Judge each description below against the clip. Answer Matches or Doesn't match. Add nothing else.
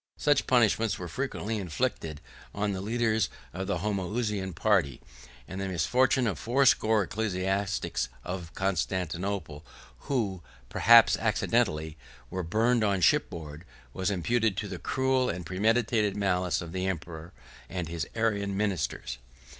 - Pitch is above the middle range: Doesn't match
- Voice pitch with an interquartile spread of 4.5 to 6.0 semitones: Doesn't match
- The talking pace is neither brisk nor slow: Doesn't match